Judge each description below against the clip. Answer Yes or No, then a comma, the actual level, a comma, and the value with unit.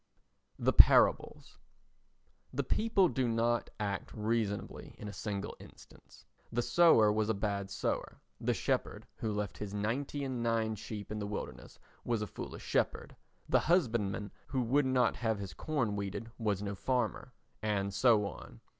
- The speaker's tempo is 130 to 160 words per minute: Yes, average, 155 wpm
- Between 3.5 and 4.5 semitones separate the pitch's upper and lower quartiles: No, average, 2.9 semitones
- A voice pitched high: No, low, 110 Hz